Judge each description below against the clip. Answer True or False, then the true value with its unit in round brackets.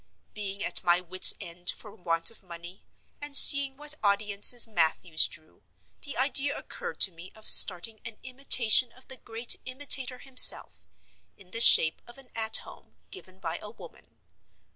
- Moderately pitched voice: False (215 Hz)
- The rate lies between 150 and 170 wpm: True (165 wpm)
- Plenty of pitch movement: True (6.0 semitones)